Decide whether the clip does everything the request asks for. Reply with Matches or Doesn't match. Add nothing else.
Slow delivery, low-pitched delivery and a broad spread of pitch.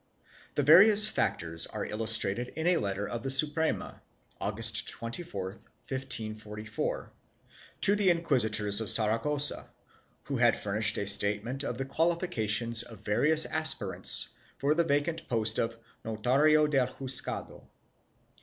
Matches